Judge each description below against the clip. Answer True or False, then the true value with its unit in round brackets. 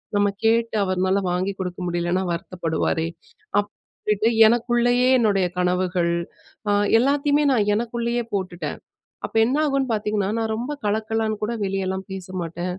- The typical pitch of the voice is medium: False (205 Hz)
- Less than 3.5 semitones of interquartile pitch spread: False (4.0 semitones)